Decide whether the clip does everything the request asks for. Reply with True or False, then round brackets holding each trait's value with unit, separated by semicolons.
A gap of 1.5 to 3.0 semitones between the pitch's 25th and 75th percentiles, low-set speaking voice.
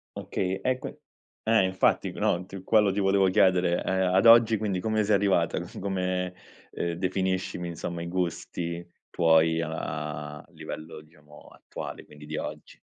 True (2.7 semitones; 90 Hz)